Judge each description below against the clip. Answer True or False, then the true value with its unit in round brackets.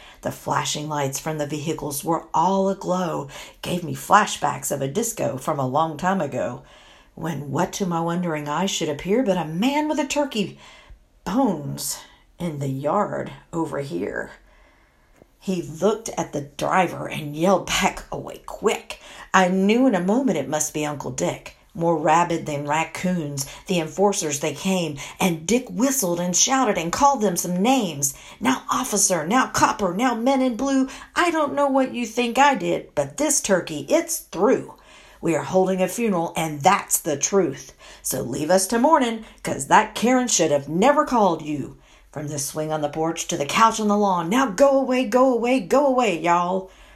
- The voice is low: False (185 Hz)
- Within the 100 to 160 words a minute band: False (180 wpm)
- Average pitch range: False (7.0 semitones)